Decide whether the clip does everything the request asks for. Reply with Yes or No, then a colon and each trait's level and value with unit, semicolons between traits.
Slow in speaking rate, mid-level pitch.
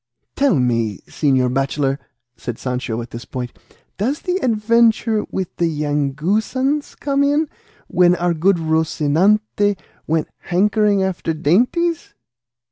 Yes: slow, 120 wpm; medium, 175 Hz